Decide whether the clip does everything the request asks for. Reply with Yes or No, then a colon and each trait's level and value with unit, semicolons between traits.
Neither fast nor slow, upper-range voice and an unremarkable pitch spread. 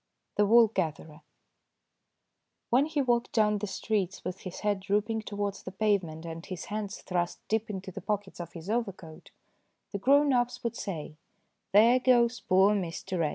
Yes: average, 165 wpm; high, 205 Hz; average, 3.7 semitones